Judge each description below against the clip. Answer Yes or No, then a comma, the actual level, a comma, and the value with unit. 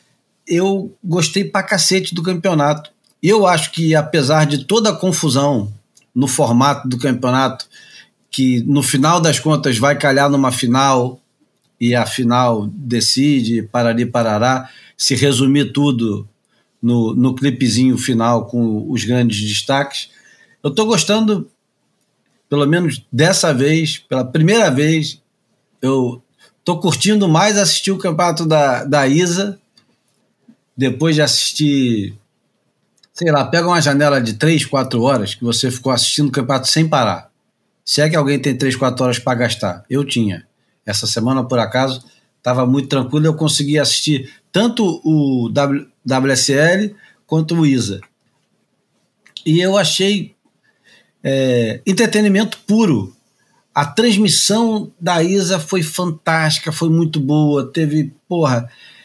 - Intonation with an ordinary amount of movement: Yes, average, 5.0 semitones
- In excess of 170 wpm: No, average, 130 wpm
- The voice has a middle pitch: Yes, medium, 145 Hz